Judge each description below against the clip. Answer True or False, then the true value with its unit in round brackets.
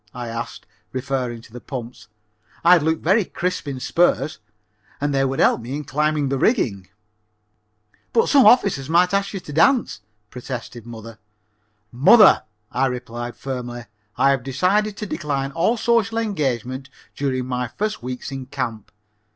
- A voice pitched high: False (135 Hz)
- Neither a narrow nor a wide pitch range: False (6.3 semitones)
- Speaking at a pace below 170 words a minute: True (160 wpm)